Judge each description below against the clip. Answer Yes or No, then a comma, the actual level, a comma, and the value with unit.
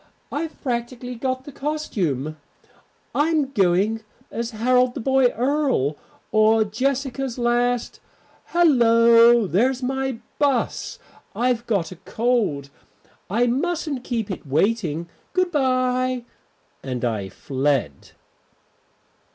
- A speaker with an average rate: No, slow, 100 wpm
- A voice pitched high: Yes, high, 240 Hz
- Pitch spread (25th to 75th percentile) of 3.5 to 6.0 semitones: Yes, average, 4.4 semitones